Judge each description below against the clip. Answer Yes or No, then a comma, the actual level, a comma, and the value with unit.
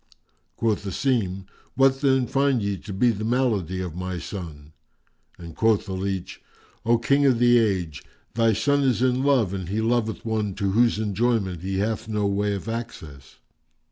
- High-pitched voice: No, low, 110 Hz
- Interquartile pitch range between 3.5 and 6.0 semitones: Yes, average, 4.1 semitones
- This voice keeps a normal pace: Yes, average, 175 wpm